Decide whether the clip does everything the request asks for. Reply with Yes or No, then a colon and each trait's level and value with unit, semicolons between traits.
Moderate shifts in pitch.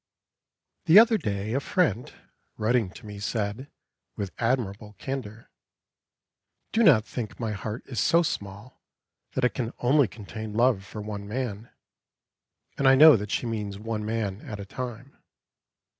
Yes: average, 3.8 semitones